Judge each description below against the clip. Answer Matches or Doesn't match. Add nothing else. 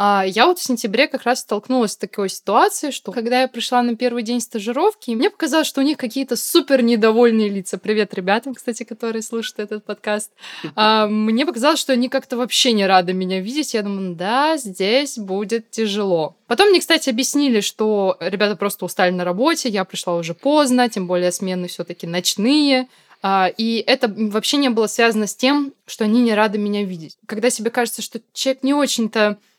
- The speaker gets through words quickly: Matches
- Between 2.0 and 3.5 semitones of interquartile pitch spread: Doesn't match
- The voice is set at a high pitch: Matches